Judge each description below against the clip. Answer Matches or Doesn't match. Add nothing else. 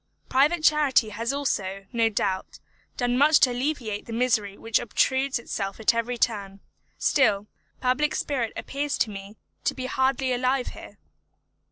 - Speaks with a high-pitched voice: Matches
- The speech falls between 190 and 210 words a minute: Doesn't match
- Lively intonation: Doesn't match